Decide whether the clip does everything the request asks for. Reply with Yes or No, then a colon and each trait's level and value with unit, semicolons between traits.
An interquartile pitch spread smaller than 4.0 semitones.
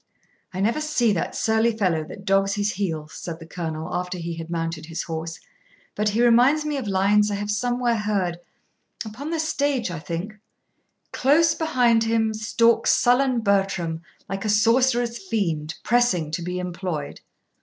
No: wide, 5.4 semitones